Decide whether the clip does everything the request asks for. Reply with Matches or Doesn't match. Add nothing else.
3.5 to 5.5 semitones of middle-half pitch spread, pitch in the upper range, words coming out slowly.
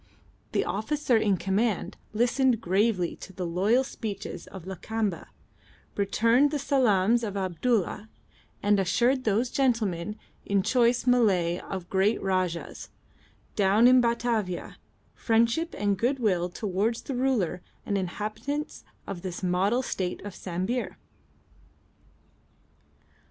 Matches